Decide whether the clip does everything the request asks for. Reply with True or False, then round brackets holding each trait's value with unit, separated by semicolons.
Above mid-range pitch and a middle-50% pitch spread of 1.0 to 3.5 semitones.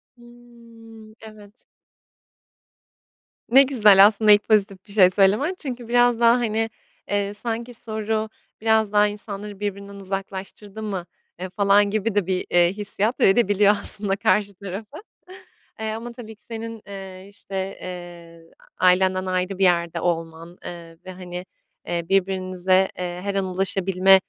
True (200 Hz; 2.8 semitones)